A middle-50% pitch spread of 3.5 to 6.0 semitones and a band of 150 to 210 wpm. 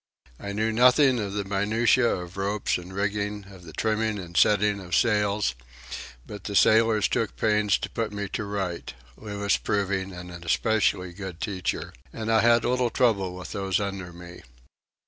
No: average, 2.9 semitones; average, 160 wpm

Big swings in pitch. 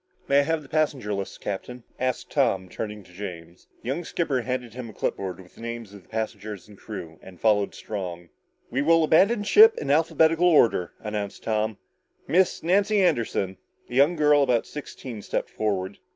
Yes: wide, 6.9 semitones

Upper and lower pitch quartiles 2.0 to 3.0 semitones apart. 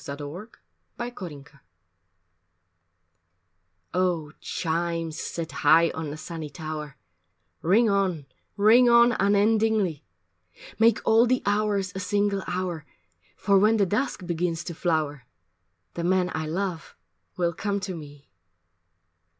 No: average, 4.3 semitones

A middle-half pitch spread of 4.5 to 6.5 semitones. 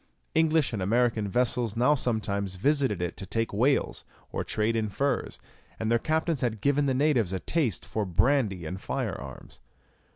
Yes: wide, 5.6 semitones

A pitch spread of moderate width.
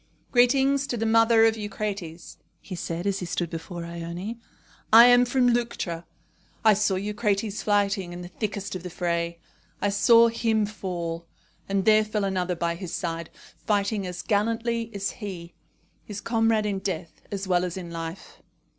Yes: average, 4.1 semitones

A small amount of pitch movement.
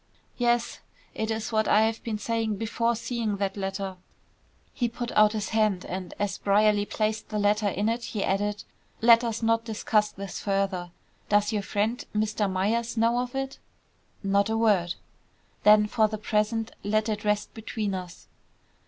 Yes: narrow, 1.8 semitones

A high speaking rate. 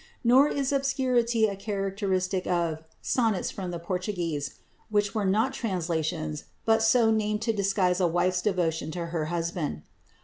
No: average, 145 wpm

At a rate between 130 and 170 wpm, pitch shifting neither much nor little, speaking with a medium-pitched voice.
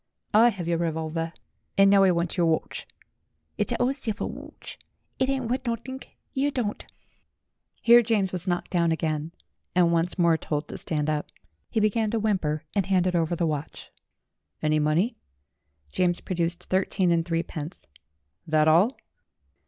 Yes: average, 160 wpm; average, 4.6 semitones; medium, 175 Hz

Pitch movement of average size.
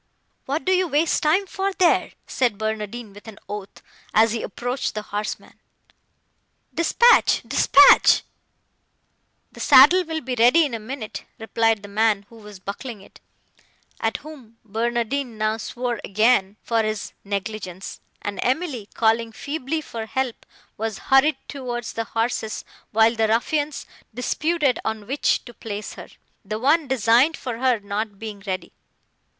Yes: average, 4.0 semitones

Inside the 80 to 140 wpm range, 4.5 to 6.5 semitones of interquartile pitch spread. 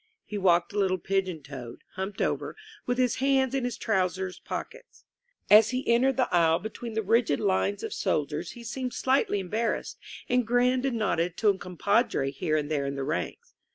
No: average, 195 wpm; wide, 5.5 semitones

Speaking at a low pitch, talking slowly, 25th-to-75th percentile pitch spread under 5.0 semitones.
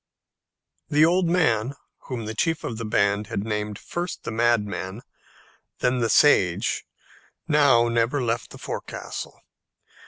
No: low, 115 Hz; slow, 130 wpm; average, 5.3 semitones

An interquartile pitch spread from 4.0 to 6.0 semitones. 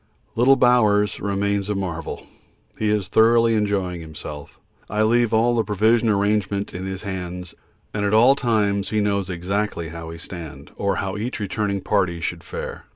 No: average, 3.0 semitones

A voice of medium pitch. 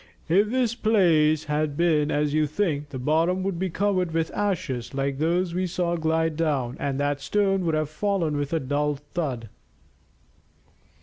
Yes: medium, 160 Hz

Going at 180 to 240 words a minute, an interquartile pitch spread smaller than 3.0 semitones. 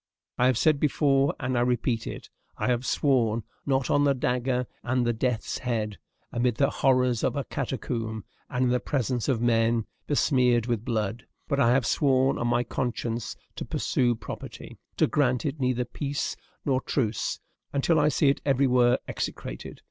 No: average, 170 wpm; narrow, 2.4 semitones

